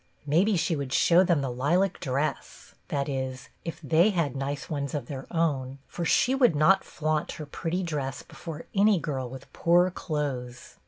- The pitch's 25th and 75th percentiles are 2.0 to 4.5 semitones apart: Yes, average, 4.1 semitones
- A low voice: No, medium, 150 Hz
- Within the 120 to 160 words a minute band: No, average, 180 wpm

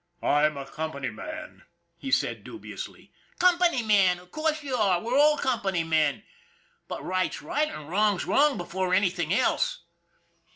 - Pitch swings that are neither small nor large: No, wide, 8.9 semitones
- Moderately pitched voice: No, high, 200 Hz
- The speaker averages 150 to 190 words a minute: Yes, average, 155 wpm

